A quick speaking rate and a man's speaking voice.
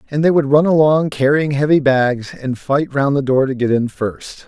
Yes: fast, 230 wpm; male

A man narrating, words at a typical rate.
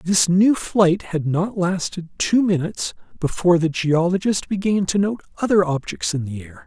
Yes: male; average, 170 wpm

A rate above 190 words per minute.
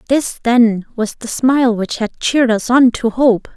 Yes: average, 200 wpm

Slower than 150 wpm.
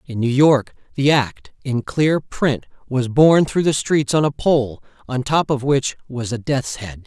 No: average, 185 wpm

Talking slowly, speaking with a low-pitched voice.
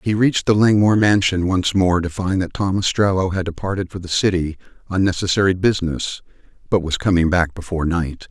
No: average, 190 wpm; very low, 90 Hz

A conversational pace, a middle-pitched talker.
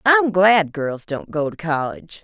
Yes: average, 190 wpm; medium, 175 Hz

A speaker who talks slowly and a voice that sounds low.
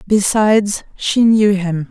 No: slow, 125 wpm; high, 205 Hz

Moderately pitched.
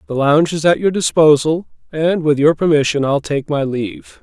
Yes: medium, 150 Hz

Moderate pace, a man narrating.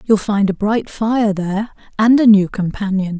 No: average, 190 wpm; female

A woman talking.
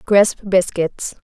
Yes: female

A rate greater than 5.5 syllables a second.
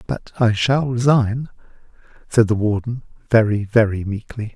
No: 4.6 syllables/s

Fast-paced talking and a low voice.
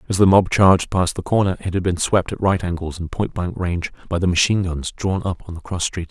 Yes: fast, 275 wpm; very low, 90 Hz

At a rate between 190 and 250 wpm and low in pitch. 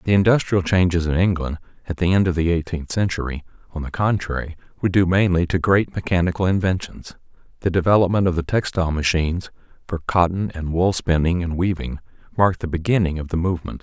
No: average, 180 wpm; very low, 85 Hz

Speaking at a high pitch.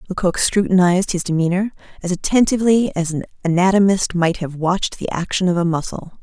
No: medium, 180 Hz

